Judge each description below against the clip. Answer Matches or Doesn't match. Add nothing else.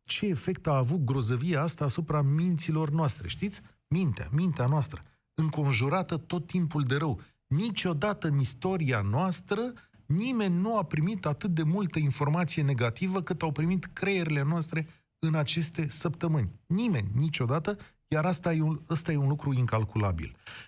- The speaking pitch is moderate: Matches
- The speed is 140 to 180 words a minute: Matches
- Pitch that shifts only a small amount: Doesn't match